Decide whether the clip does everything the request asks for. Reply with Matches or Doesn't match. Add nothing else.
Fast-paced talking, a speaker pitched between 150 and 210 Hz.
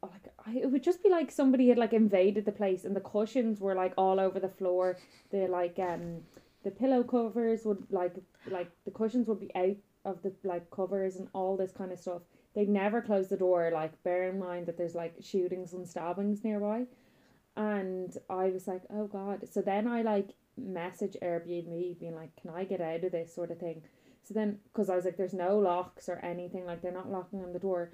Matches